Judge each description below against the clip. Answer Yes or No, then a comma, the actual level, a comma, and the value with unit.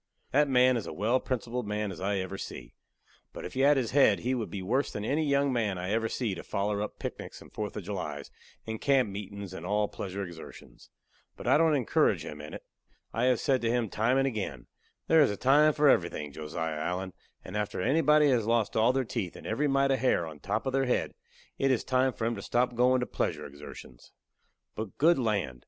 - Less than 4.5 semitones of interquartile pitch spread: No, average, 5.1 semitones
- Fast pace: Yes, fast, 230 wpm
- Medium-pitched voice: No, low, 115 Hz